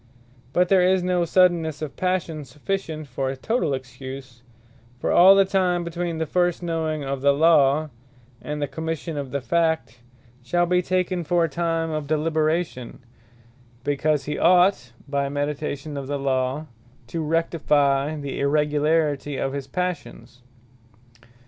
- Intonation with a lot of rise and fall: No, average, 3.6 semitones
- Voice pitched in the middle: Yes, medium, 155 Hz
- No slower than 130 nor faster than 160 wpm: Yes, average, 145 wpm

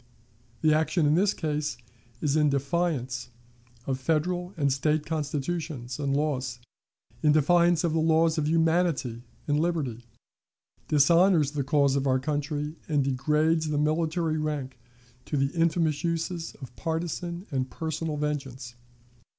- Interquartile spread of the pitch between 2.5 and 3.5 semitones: Yes, average, 2.9 semitones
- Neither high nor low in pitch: Yes, medium, 150 Hz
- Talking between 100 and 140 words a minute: Yes, slow, 135 wpm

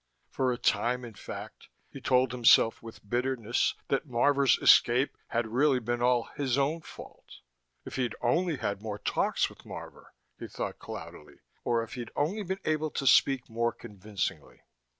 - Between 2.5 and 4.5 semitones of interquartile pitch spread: Yes, average, 2.9 semitones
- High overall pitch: No, low, 125 Hz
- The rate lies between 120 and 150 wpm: No, average, 165 wpm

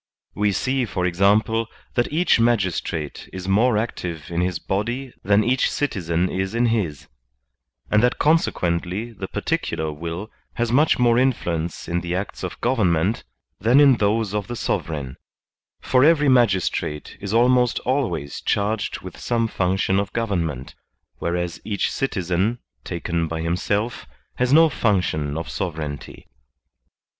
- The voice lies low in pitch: Yes, low, 100 Hz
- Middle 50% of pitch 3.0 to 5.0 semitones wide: No, wide, 5.5 semitones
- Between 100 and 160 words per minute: Yes, average, 140 wpm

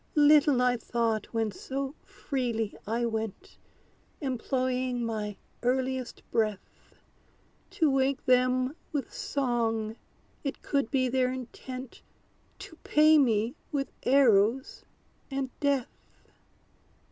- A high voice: Yes, very high, 255 Hz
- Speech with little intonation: No, average, 3.1 semitones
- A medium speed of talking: No, slow, 100 wpm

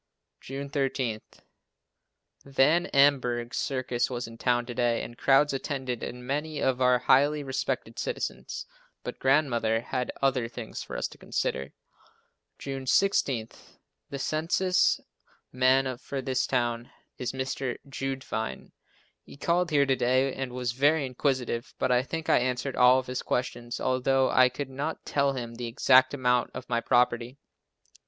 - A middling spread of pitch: No, narrow, 2.0 semitones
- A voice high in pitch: No, low, 130 Hz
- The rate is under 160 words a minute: Yes, average, 150 wpm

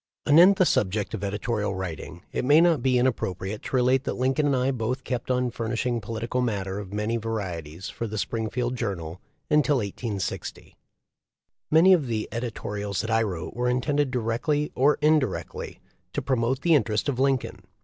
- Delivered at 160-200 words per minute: Yes, average, 170 wpm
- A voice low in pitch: Yes, low, 120 Hz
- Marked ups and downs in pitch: No, average, 4.2 semitones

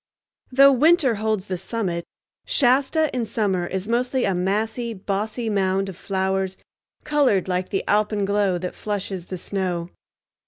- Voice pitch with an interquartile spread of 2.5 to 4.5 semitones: Yes, average, 3.8 semitones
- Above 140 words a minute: No, slow, 135 wpm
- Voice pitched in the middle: No, high, 200 Hz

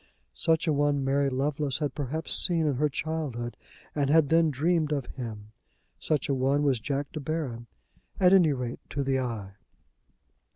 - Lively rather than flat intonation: No, average, 3.1 semitones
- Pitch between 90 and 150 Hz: Yes, medium, 140 Hz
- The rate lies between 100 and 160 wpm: No, average, 170 wpm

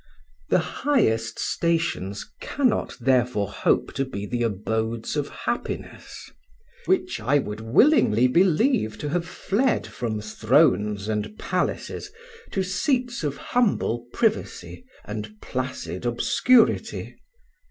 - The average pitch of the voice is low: Yes, low, 130 Hz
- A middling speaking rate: No, slow, 110 wpm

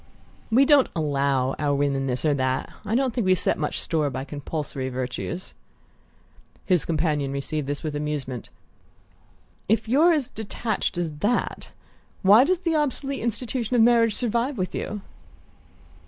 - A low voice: No, medium, 170 Hz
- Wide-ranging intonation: Yes, wide, 8.9 semitones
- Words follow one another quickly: No, average, 155 wpm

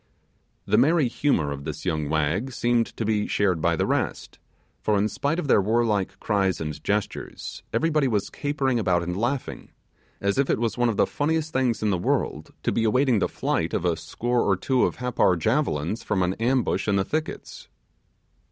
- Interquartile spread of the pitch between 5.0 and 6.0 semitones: Yes, wide, 5.6 semitones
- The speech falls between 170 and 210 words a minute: Yes, average, 190 wpm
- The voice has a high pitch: No, low, 110 Hz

